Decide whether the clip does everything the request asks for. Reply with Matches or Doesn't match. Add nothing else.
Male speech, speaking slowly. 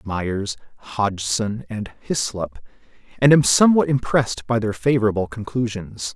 Matches